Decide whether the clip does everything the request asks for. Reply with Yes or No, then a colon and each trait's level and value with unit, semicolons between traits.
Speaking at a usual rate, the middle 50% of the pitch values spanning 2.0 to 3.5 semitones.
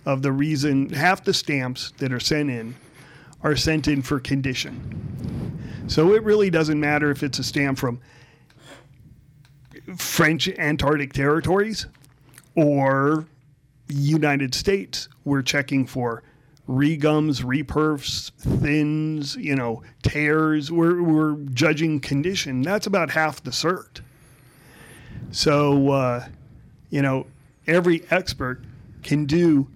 No: slow, 115 wpm; narrow, 2.4 semitones